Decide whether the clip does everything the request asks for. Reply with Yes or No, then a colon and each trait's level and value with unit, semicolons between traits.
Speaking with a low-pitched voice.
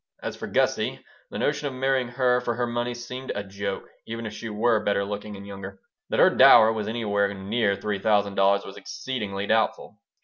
Yes: low, 105 Hz